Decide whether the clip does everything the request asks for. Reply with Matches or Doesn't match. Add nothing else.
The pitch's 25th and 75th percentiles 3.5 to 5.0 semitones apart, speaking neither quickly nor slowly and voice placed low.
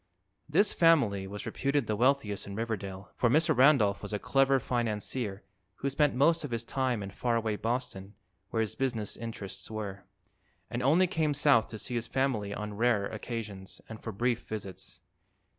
Matches